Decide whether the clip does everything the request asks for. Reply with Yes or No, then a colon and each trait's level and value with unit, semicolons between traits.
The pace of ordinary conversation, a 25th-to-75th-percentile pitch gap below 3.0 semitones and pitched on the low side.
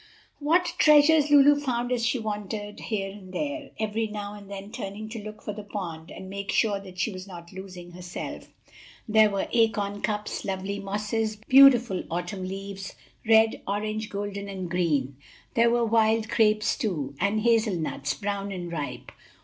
No: average, 165 wpm; narrow, 2.6 semitones; high, 205 Hz